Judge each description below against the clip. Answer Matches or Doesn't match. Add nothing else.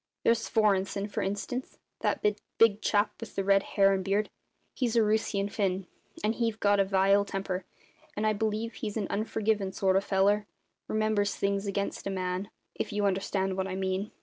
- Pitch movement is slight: Matches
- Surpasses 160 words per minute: Matches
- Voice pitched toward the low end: Doesn't match